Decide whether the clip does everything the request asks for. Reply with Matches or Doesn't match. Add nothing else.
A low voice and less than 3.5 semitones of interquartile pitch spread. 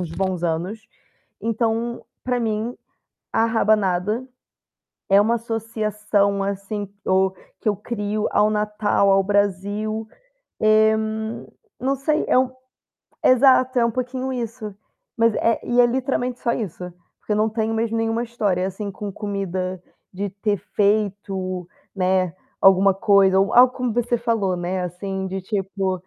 Doesn't match